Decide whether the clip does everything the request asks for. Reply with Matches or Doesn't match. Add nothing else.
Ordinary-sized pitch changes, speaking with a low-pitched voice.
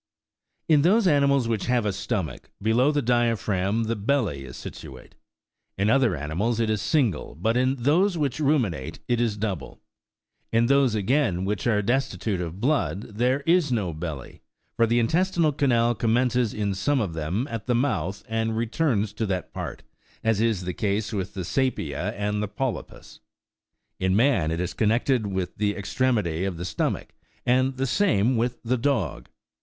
Matches